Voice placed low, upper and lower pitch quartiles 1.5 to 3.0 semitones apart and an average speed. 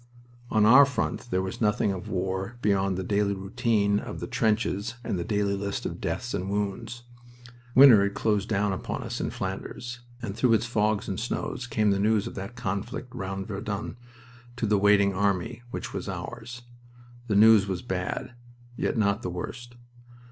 Yes: low, 105 Hz; average, 2.7 semitones; average, 175 wpm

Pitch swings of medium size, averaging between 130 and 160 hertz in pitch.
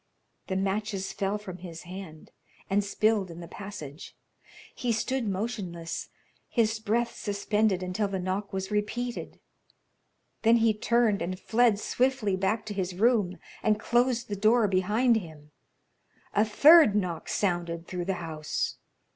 No: average, 3.3 semitones; high, 205 Hz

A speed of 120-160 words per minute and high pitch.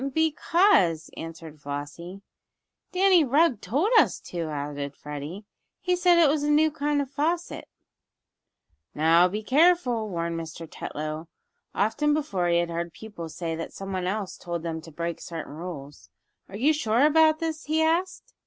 Yes: average, 155 wpm; high, 195 Hz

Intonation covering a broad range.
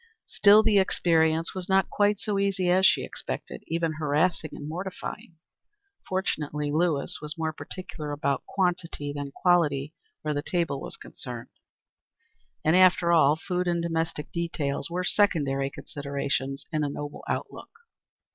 No: average, 3.8 semitones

